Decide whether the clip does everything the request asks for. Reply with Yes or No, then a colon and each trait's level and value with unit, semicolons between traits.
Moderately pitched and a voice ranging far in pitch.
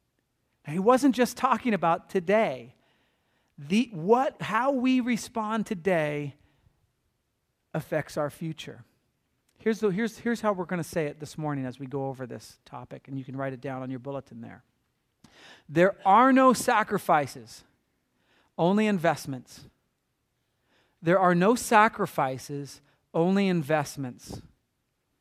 Yes: medium, 165 Hz; wide, 7.7 semitones